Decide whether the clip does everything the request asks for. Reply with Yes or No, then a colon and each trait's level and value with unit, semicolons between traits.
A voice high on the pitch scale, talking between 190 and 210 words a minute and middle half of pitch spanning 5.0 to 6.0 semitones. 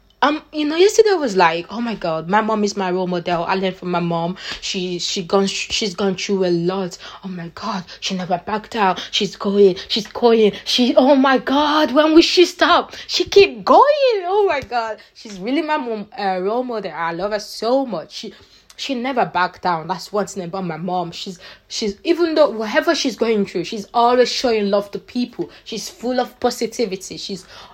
Yes: high, 215 Hz; fast, 205 wpm; average, 5.3 semitones